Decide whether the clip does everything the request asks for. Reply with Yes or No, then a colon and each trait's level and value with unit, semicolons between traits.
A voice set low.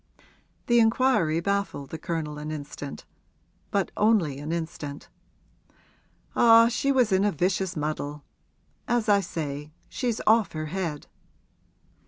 No: medium, 175 Hz